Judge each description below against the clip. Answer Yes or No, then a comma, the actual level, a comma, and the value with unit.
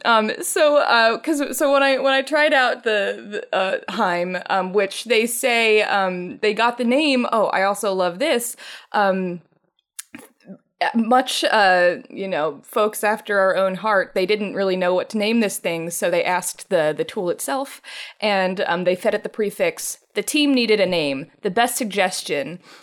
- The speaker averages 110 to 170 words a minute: No, average, 185 wpm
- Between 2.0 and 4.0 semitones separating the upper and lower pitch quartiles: No, average, 4.7 semitones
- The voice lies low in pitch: No, high, 210 Hz